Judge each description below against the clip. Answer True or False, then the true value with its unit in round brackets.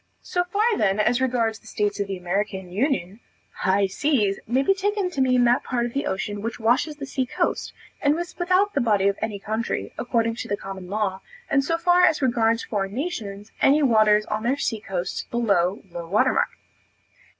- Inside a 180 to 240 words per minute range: True (200 wpm)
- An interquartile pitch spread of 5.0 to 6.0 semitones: True (5.6 semitones)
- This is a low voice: False (230 Hz)